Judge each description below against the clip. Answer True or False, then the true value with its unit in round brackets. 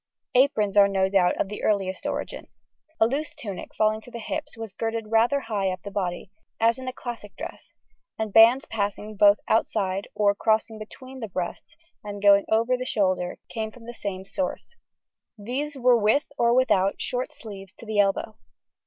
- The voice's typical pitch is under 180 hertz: False (215 Hz)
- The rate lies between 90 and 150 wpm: False (180 wpm)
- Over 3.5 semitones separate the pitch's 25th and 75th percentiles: False (3.2 semitones)